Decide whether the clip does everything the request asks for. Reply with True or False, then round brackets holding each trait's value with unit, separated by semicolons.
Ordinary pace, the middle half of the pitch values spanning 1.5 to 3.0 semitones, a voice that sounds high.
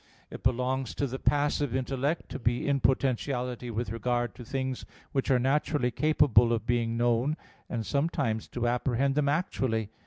False (160 wpm; 2.6 semitones; 125 Hz)